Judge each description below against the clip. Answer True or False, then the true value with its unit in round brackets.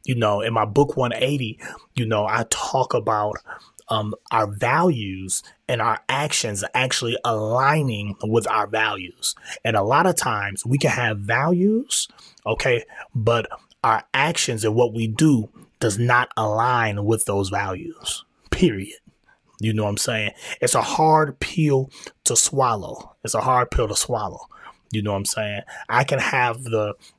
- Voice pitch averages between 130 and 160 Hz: False (115 Hz)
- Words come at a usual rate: True (160 wpm)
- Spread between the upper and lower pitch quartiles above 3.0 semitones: True (3.7 semitones)